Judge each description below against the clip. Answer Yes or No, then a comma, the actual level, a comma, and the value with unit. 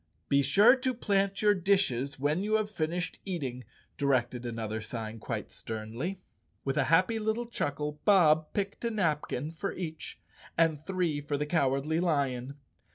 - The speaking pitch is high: No, medium, 155 Hz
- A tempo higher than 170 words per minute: No, average, 160 wpm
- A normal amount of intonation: No, wide, 6.2 semitones